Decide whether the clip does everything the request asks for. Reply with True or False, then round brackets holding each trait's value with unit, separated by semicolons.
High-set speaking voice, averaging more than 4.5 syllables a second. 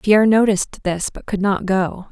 True (200 Hz; 5.0 syllables/s)